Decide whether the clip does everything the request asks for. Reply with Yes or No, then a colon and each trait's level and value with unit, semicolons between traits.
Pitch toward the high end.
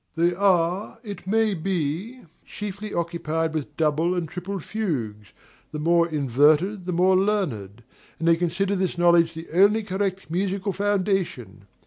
No: medium, 175 Hz